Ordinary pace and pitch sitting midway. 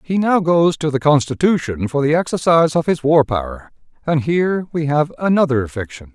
Yes: average, 185 wpm; medium, 150 Hz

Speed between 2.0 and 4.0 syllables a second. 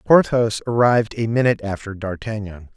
No: 5.5 syllables/s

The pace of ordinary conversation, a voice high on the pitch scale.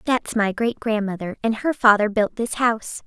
Yes: average, 195 wpm; high, 220 Hz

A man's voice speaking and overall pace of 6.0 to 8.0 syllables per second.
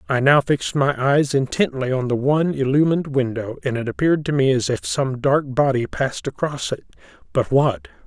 No: male; 5.4 syllables/s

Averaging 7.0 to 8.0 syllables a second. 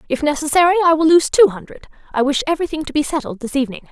Yes: 7.6 syllables/s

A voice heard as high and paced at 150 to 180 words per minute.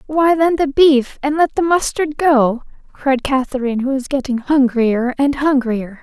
Yes: very high, 275 Hz; average, 170 wpm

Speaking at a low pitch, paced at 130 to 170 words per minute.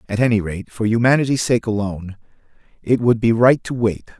No: low, 110 Hz; average, 185 wpm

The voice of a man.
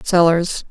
No: female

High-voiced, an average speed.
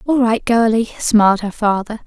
Yes: high, 220 Hz; average, 175 wpm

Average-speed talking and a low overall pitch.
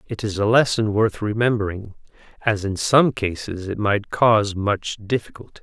Yes: average, 160 wpm; low, 105 Hz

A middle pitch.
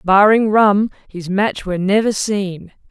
No: high, 200 Hz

